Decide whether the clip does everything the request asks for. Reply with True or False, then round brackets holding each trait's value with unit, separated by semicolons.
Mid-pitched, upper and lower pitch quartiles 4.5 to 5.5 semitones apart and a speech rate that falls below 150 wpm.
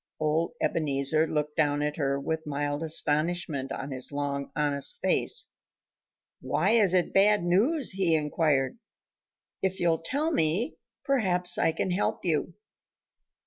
False (160 Hz; 3.9 semitones; 135 wpm)